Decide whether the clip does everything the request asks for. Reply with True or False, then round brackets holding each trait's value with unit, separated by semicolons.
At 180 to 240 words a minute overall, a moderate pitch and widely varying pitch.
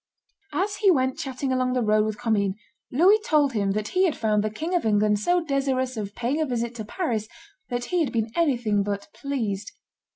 False (205 wpm; 245 Hz; 5.8 semitones)